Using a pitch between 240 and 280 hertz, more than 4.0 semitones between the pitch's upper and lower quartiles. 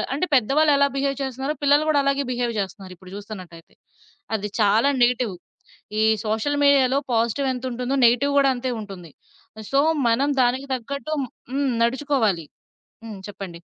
Yes: very high, 250 Hz; average, 4.7 semitones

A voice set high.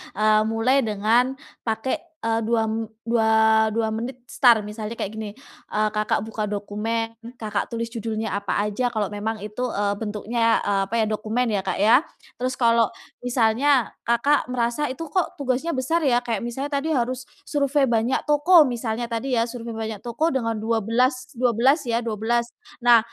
Yes: high, 230 Hz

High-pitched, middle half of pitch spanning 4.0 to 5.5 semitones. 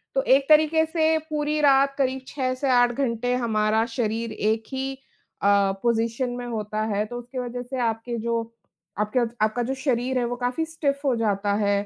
No: high, 245 Hz; average, 3.3 semitones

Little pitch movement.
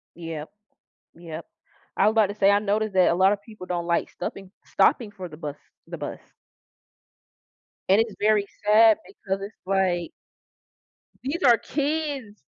No: average, 3.2 semitones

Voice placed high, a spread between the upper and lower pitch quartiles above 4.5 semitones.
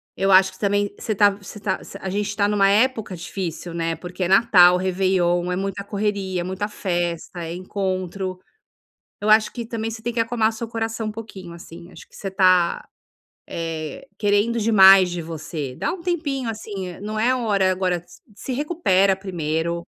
No: high, 195 Hz; average, 3.3 semitones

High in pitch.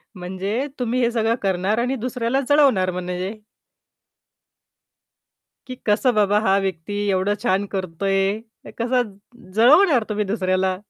Yes: high, 205 Hz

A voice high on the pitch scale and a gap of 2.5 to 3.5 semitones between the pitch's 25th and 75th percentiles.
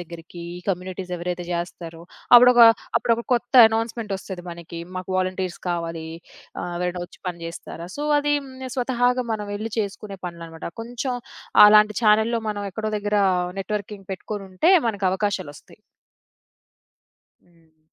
No: high, 195 Hz; average, 4.0 semitones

